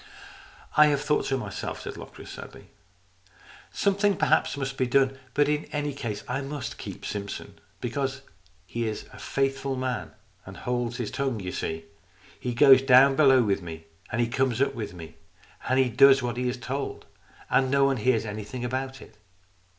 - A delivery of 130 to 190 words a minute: Yes, average, 185 wpm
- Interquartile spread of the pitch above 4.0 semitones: No, average, 3.0 semitones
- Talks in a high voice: No, low, 130 Hz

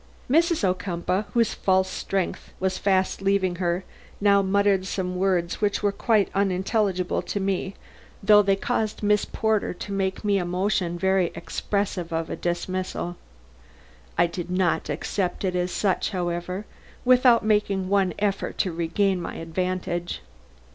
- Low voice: No, high, 190 Hz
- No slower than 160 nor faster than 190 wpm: No, average, 145 wpm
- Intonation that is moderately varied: No, narrow, 2.0 semitones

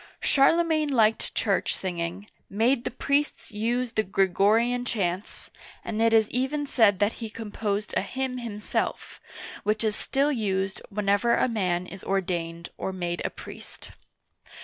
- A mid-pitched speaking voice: No, high, 215 Hz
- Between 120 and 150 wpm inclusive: Yes, average, 145 wpm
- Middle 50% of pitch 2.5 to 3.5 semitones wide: No, average, 4.0 semitones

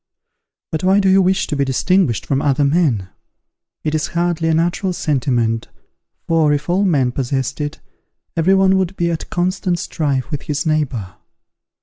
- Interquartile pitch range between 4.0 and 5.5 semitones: Yes, average, 4.4 semitones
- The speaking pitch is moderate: Yes, medium, 155 Hz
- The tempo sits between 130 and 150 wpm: No, average, 165 wpm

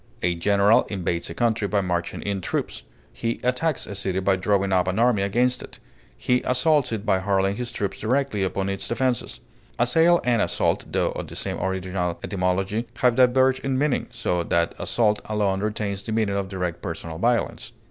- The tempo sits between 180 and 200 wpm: Yes, average, 185 wpm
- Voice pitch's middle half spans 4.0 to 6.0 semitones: Yes, average, 4.3 semitones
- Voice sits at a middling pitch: No, low, 100 Hz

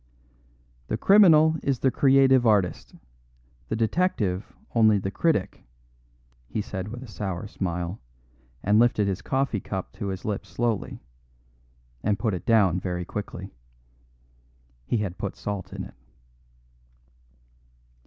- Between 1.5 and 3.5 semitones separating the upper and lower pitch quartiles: No, average, 4.2 semitones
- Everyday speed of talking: No, slow, 125 wpm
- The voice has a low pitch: Yes, low, 105 Hz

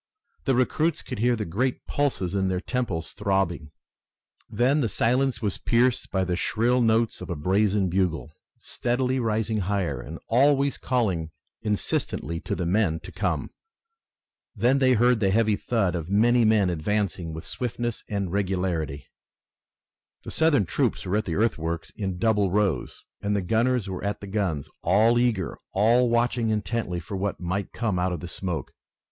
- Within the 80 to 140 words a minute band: No, average, 165 wpm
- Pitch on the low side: Yes, low, 105 Hz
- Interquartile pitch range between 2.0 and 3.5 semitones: No, average, 4.6 semitones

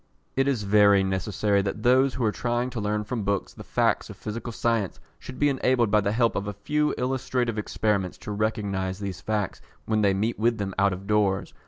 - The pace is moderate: No, fast, 210 wpm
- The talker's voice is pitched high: No, low, 105 Hz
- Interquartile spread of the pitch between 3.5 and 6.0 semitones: No, average, 3.1 semitones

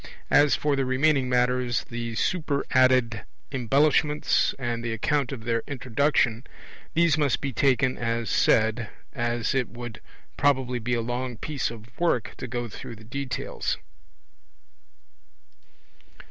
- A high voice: No, low, 125 Hz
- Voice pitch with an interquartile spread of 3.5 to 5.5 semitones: No, average, 3.0 semitones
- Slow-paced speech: Yes, slow, 130 wpm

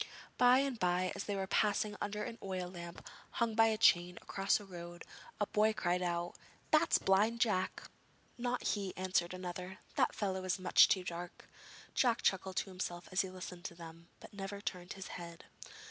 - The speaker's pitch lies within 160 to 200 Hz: Yes, high, 190 Hz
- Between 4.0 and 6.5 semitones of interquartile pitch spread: No, average, 2.9 semitones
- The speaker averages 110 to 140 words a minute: No, average, 185 wpm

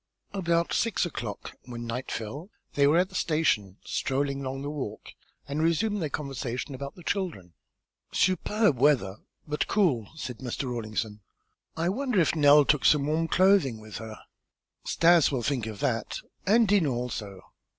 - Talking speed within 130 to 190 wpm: Yes, average, 160 wpm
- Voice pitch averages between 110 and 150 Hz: Yes, medium, 140 Hz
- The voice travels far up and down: Yes, wide, 6.1 semitones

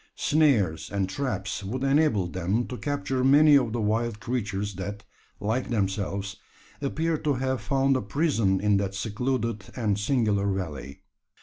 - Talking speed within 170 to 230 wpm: No, average, 145 wpm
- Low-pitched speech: Yes, low, 110 Hz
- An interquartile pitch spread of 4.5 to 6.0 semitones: Yes, average, 5.2 semitones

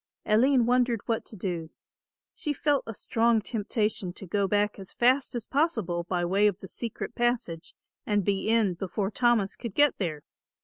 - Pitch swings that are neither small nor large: Yes, average, 3.9 semitones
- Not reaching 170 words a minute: No, average, 175 wpm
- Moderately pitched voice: No, high, 210 Hz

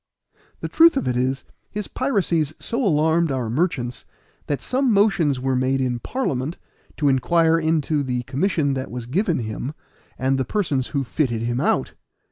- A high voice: No, medium, 145 Hz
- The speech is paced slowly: No, average, 165 wpm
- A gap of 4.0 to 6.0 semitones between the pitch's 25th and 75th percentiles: Yes, average, 4.9 semitones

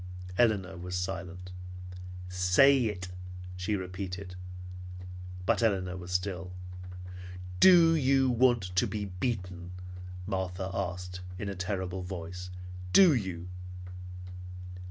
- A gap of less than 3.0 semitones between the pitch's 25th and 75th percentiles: Yes, narrow, 2.6 semitones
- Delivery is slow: Yes, slow, 100 wpm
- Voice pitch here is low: Yes, very low, 95 Hz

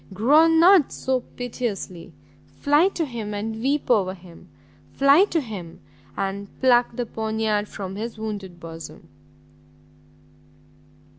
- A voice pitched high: Yes, high, 220 Hz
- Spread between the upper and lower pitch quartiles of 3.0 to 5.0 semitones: No, wide, 5.5 semitones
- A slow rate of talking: Yes, slow, 120 wpm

